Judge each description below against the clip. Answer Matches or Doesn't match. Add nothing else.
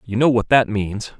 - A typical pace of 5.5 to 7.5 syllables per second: Doesn't match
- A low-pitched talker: Matches